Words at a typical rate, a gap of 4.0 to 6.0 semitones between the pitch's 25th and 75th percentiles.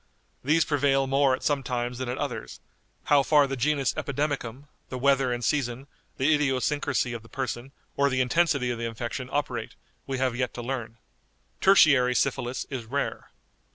No: average, 170 wpm; narrow, 2.4 semitones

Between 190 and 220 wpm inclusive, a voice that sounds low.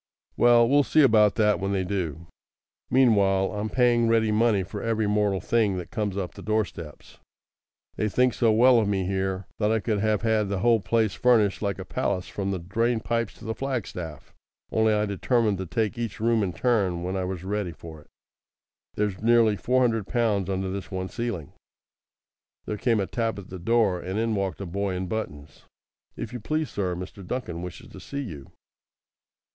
Yes: average, 200 wpm; low, 105 Hz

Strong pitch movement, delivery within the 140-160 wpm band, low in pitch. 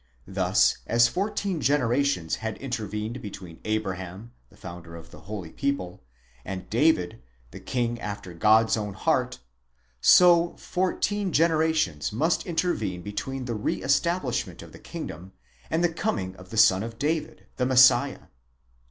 Yes: wide, 7.9 semitones; average, 145 wpm; low, 115 Hz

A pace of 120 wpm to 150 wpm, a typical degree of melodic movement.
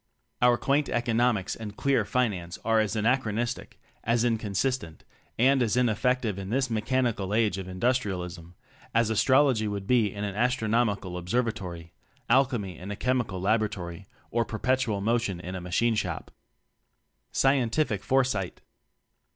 Yes: slow, 135 wpm; average, 4.0 semitones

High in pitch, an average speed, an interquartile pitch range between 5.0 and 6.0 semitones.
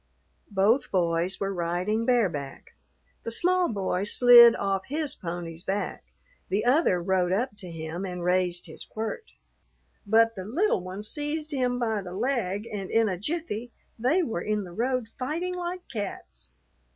Yes: high, 210 Hz; average, 155 wpm; wide, 5.5 semitones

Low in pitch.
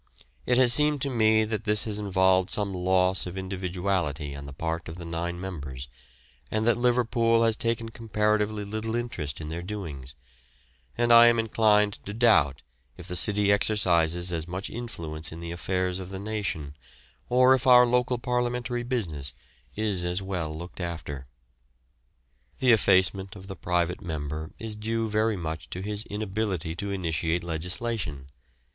Yes: very low, 95 Hz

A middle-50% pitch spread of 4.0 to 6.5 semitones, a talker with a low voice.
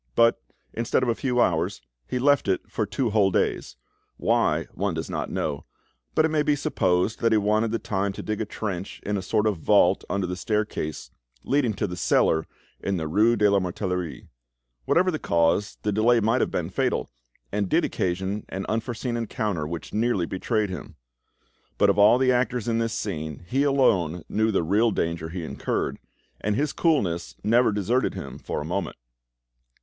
Yes: average, 4.4 semitones; low, 105 Hz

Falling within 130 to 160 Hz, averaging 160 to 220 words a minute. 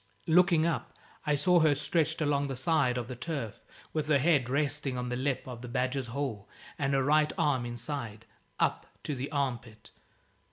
Yes: medium, 140 Hz; average, 190 wpm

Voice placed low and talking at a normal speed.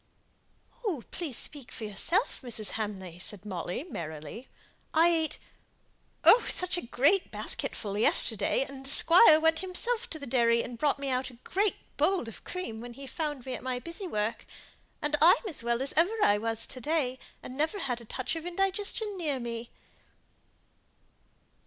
No: very high, 270 Hz; average, 165 wpm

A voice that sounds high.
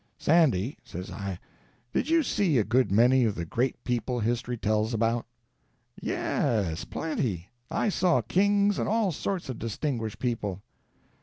No: low, 120 Hz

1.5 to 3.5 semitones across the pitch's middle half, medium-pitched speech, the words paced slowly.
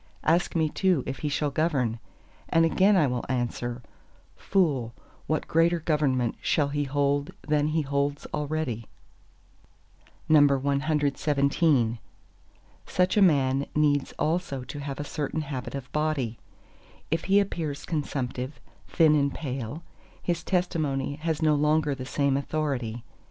Yes: average, 2.7 semitones; medium, 145 Hz; slow, 130 wpm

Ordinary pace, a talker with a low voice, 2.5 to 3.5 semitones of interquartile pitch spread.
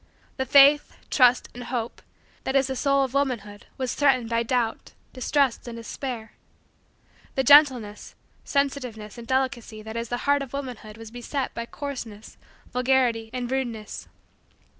No: average, 145 wpm; very high, 250 Hz; average, 2.8 semitones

